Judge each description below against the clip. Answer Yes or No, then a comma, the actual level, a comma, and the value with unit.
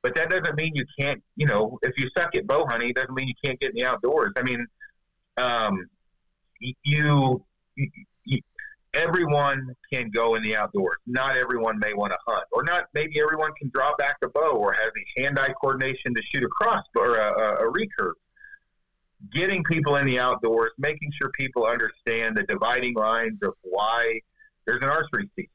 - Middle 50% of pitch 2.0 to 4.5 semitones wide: No, average, 4.9 semitones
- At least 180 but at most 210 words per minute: Yes, average, 190 wpm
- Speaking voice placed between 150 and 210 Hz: No, low, 135 Hz